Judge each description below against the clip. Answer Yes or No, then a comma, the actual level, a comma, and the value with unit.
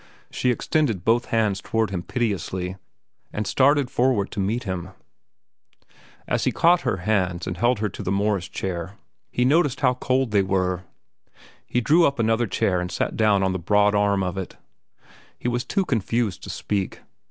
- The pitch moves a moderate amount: Yes, average, 4.5 semitones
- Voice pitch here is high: No, low, 105 Hz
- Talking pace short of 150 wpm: No, average, 175 wpm